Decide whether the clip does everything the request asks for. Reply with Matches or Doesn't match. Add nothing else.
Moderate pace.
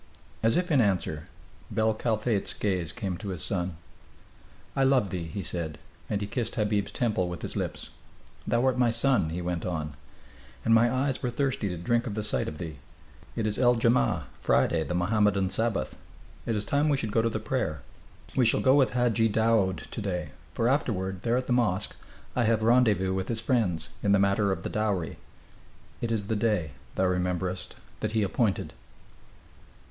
Matches